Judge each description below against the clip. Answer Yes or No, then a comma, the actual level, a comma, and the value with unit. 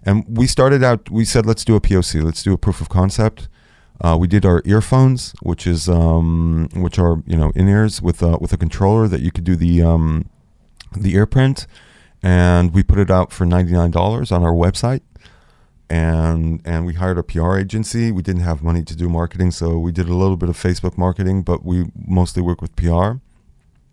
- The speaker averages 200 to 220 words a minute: Yes, fast, 205 wpm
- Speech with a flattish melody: No, average, 3.0 semitones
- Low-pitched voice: Yes, very low, 90 Hz